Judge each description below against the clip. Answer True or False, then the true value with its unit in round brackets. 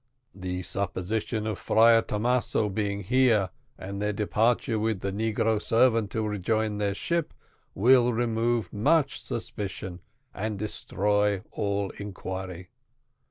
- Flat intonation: True (2.3 semitones)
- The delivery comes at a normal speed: False (115 wpm)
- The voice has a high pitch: False (105 Hz)